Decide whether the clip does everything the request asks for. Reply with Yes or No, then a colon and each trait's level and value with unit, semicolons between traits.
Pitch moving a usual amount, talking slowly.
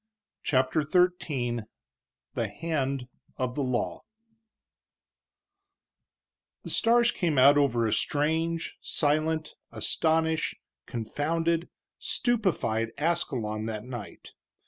Yes: average, 4.9 semitones; slow, 85 wpm